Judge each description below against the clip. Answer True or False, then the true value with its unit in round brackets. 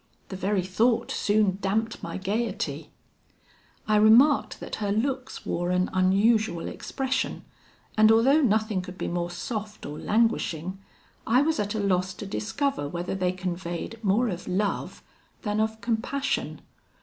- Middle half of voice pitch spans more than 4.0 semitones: False (3.6 semitones)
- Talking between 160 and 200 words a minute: False (145 wpm)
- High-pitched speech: True (210 Hz)